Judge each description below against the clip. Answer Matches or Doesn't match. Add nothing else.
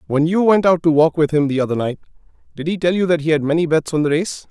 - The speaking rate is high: Matches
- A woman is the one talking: Doesn't match